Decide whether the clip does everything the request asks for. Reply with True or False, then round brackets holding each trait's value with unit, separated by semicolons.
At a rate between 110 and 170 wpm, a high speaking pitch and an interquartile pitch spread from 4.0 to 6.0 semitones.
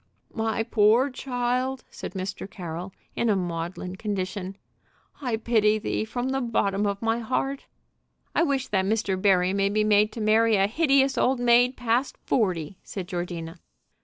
True (160 wpm; 215 Hz; 4.3 semitones)